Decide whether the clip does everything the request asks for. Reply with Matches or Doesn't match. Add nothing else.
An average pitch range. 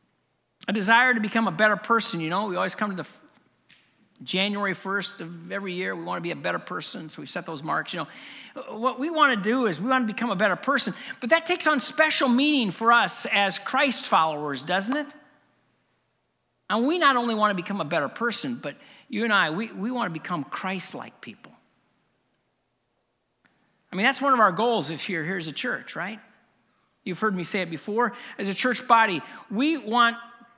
Matches